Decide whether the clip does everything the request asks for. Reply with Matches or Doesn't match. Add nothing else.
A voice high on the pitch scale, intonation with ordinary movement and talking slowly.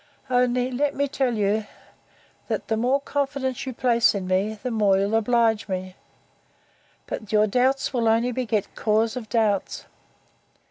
Doesn't match